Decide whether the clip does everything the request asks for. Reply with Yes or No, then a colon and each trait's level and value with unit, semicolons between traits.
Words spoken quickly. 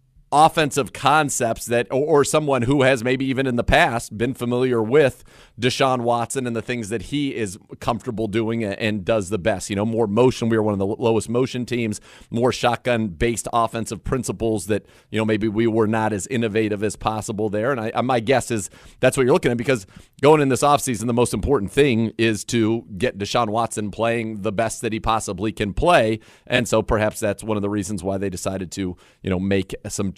Yes: fast, 215 wpm